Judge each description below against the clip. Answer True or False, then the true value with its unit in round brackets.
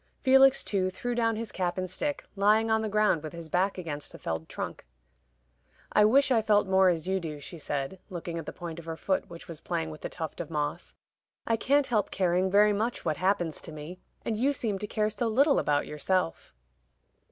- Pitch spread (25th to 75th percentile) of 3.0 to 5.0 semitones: True (4.7 semitones)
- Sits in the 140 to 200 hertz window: True (190 Hz)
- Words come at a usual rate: False (220 wpm)